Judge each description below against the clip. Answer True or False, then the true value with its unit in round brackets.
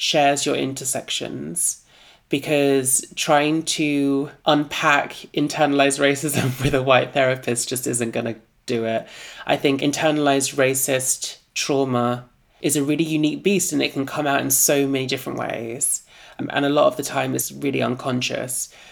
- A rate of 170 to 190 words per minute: False (150 wpm)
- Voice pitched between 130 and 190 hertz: True (140 Hz)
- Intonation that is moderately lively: False (2.1 semitones)